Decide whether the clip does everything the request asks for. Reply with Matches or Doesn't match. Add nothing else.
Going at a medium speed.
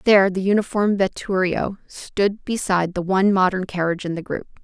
Matches